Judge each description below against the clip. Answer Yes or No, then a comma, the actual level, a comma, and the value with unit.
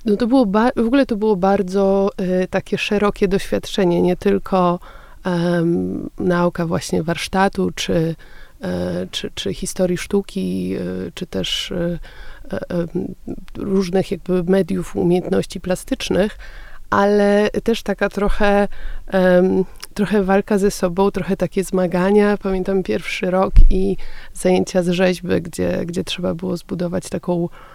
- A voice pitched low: No, high, 190 Hz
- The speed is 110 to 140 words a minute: Yes, average, 130 wpm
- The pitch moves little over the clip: Yes, narrow, 2.1 semitones